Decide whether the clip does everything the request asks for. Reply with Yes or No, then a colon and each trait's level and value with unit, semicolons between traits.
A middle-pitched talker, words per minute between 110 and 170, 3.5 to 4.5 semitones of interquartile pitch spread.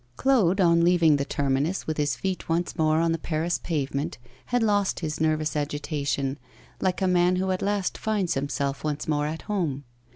No: medium, 165 Hz; average, 185 wpm; average, 3.9 semitones